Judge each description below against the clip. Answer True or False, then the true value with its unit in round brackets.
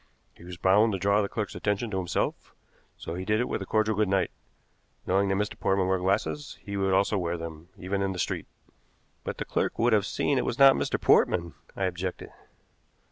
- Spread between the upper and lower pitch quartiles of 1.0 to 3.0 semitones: True (2.4 semitones)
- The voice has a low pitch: True (95 Hz)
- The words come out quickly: True (215 wpm)